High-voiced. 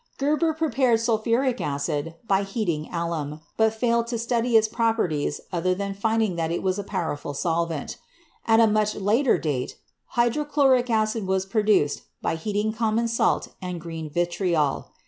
Yes: high, 210 Hz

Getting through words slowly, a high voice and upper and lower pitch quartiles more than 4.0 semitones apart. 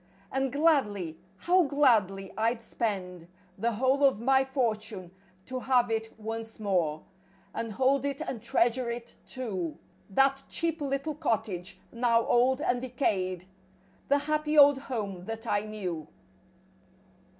Yes: slow, 130 wpm; high, 235 Hz; average, 4.8 semitones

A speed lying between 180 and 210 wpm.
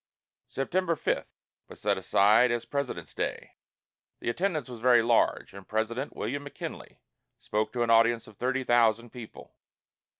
No: average, 145 wpm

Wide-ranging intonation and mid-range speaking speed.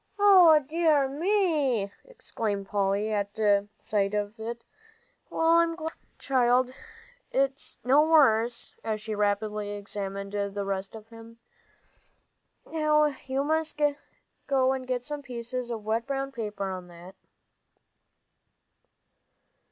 No: wide, 6.0 semitones; slow, 110 wpm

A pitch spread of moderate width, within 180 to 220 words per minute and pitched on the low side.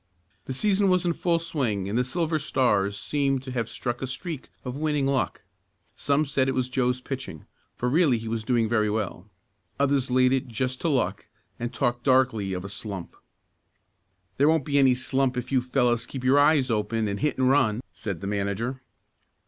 Yes: average, 3.5 semitones; average, 195 wpm; low, 130 Hz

